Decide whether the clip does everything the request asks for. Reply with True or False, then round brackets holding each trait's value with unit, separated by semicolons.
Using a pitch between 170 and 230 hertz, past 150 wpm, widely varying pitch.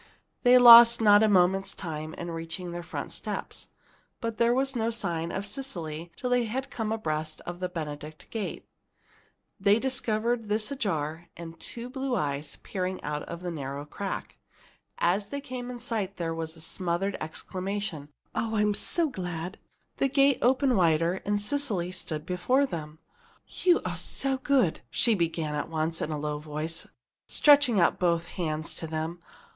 True (185 Hz; 165 wpm; 6.2 semitones)